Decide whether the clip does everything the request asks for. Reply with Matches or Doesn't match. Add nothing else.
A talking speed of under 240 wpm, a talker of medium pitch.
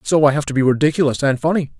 Doesn't match